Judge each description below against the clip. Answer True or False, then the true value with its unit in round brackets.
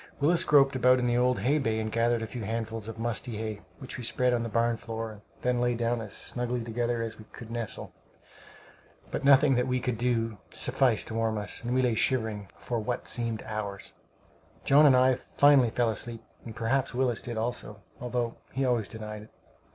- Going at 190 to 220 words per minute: True (205 wpm)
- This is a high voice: False (120 Hz)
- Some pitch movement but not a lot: False (2.0 semitones)